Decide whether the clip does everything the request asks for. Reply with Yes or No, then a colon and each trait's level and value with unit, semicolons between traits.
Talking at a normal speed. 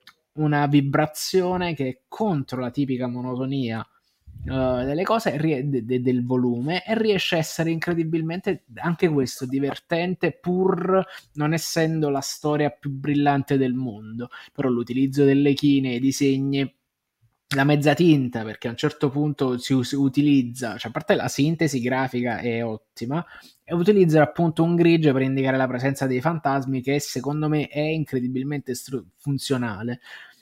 Yes: average, 145 wpm